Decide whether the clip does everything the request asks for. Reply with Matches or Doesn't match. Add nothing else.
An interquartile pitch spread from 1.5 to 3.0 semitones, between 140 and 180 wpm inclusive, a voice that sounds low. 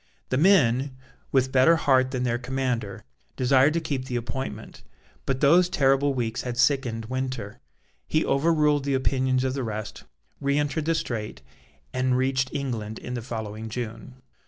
Matches